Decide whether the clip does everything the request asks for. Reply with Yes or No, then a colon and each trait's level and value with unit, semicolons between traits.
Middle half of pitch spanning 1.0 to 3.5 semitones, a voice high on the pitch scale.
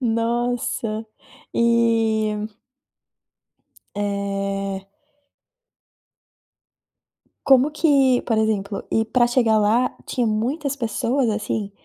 Yes: narrow, 2.5 semitones; high, 225 Hz